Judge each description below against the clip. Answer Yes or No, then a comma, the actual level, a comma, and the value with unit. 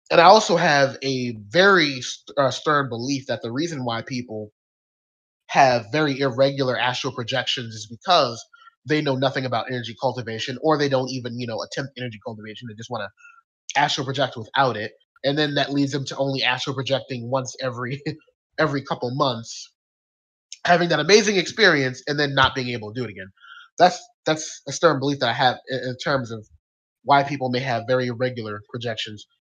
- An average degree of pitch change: Yes, average, 3.1 semitones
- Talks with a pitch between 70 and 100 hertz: No, low, 130 Hz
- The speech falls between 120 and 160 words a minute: No, average, 185 wpm